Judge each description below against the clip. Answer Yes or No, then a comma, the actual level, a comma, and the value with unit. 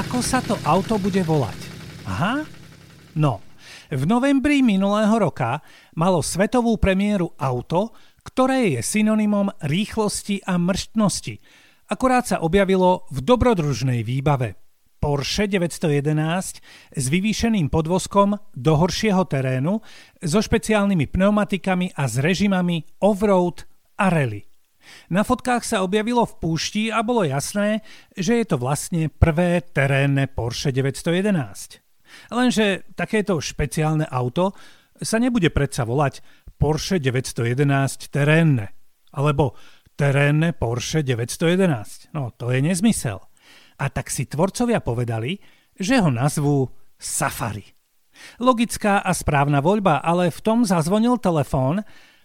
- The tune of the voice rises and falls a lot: Yes, wide, 6.7 semitones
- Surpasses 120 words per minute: No, average, 115 wpm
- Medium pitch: Yes, medium, 170 Hz